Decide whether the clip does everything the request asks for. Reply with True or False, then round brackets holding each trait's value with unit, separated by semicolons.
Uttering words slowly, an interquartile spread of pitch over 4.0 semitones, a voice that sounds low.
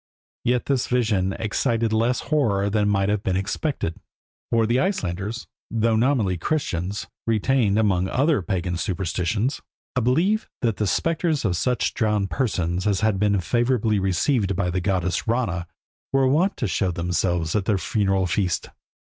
False (155 wpm; 4.5 semitones; 105 Hz)